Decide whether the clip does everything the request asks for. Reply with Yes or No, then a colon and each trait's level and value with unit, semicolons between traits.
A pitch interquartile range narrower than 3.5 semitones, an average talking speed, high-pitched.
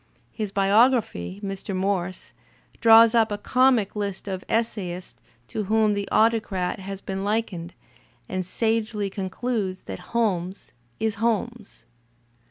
No: average, 2.9 semitones; slow, 130 wpm; high, 205 Hz